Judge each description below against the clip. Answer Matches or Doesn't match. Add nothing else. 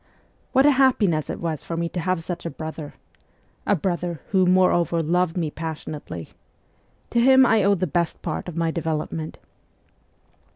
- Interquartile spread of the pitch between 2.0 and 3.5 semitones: Matches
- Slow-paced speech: Doesn't match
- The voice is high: Doesn't match